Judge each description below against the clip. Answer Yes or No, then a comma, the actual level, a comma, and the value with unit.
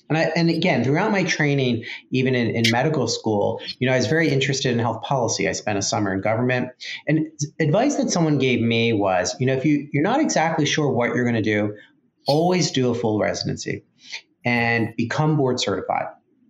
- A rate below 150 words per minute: No, fast, 205 wpm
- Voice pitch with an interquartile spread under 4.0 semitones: No, average, 5.0 semitones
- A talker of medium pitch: No, low, 130 Hz